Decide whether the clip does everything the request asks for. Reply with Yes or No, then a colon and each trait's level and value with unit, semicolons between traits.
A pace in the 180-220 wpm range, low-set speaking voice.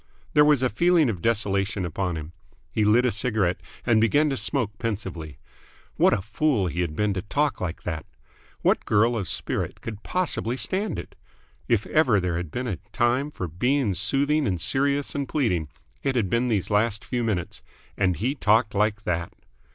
Yes: average, 185 wpm; low, 110 Hz